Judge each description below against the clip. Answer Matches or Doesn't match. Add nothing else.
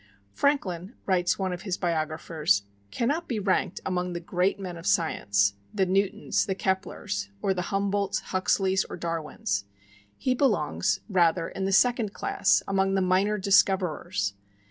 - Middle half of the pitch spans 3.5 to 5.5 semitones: Doesn't match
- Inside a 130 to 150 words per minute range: Matches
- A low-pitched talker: Doesn't match